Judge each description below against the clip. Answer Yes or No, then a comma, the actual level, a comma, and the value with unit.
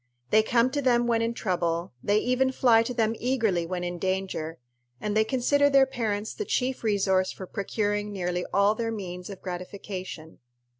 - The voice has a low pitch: No, high, 210 Hz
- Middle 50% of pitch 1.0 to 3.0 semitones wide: No, average, 4.4 semitones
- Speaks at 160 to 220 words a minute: Yes, average, 180 wpm